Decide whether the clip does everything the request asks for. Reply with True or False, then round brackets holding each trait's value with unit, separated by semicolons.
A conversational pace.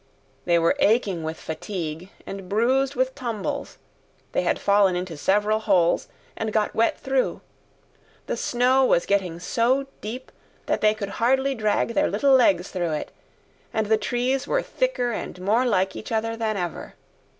True (160 wpm)